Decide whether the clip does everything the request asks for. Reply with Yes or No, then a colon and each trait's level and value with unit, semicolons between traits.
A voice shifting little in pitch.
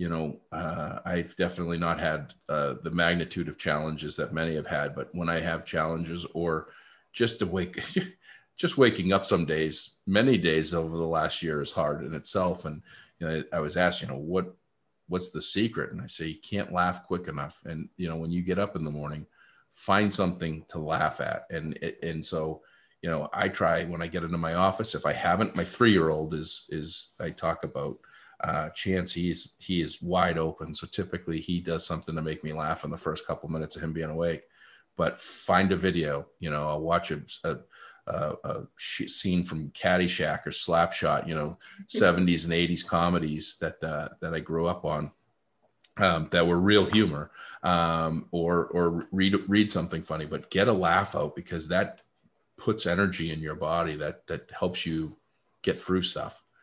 Yes: narrow, 2.2 semitones